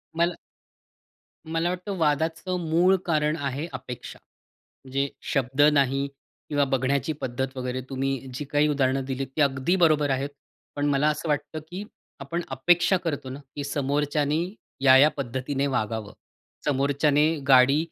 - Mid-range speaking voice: Yes, medium, 145 Hz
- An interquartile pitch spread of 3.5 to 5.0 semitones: No, narrow, 2.6 semitones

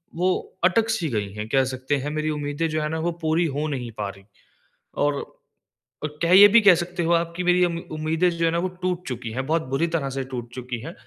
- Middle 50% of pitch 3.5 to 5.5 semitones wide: Yes, average, 4.6 semitones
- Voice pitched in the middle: Yes, medium, 155 Hz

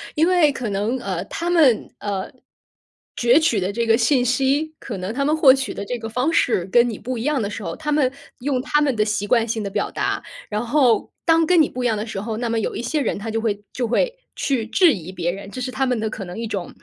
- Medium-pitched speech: No, high, 235 Hz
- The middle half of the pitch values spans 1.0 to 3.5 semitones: No, average, 4.7 semitones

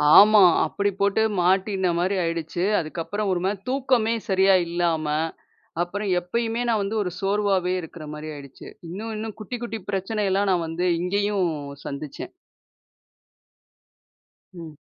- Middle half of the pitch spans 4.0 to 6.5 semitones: No, average, 3.3 semitones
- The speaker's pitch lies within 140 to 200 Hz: Yes, high, 190 Hz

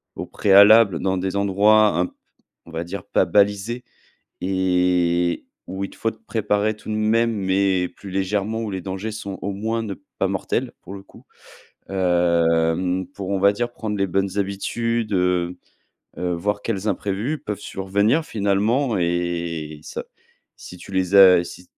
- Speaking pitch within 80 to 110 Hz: Yes, very low, 95 Hz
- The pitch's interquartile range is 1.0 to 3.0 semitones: Yes, average, 2.7 semitones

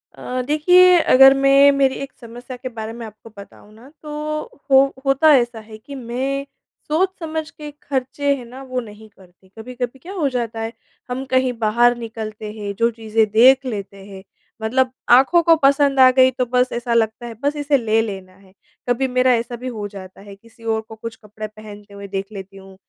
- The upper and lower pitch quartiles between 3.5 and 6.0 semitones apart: Yes, average, 3.9 semitones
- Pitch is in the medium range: No, high, 240 Hz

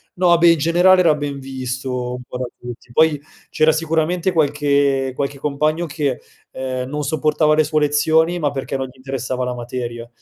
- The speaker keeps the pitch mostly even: No, average, 3.4 semitones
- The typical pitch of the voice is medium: Yes, medium, 145 Hz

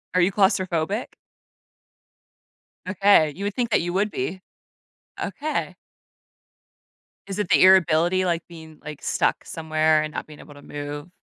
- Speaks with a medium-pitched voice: Yes, medium, 175 Hz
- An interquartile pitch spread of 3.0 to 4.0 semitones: Yes, average, 3.7 semitones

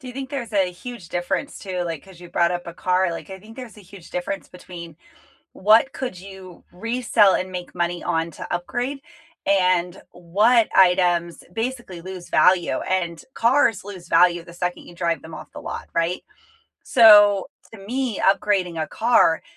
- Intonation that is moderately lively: Yes, average, 3.8 semitones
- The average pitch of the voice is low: No, medium, 185 Hz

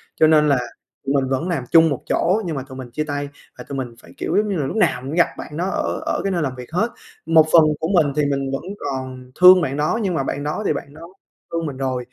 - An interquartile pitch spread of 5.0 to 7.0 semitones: No, average, 3.8 semitones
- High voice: No, medium, 150 Hz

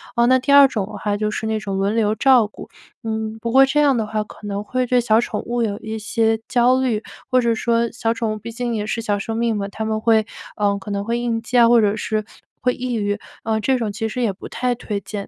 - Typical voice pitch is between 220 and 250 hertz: Yes, high, 225 Hz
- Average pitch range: No, narrow, 2.2 semitones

